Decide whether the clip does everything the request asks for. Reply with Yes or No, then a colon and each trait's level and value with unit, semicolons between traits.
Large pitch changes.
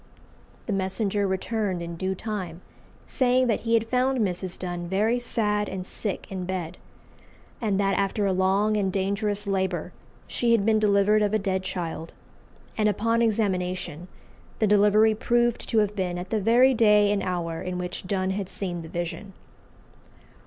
No: average, 2.8 semitones